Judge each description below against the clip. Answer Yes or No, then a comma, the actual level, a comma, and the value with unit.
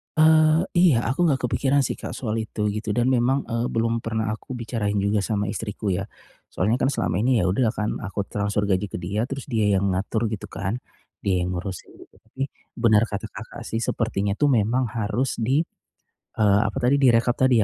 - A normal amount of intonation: Yes, average, 3.8 semitones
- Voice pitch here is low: Yes, low, 110 Hz